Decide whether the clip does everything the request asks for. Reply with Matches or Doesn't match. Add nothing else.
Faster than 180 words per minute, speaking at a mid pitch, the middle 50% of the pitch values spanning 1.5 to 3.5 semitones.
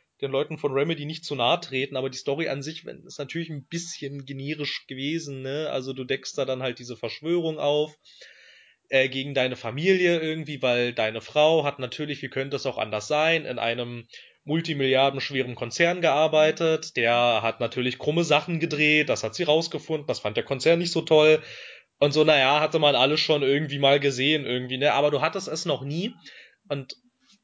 Matches